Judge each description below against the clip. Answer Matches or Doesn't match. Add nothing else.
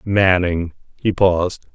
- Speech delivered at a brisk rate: Doesn't match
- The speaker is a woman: Doesn't match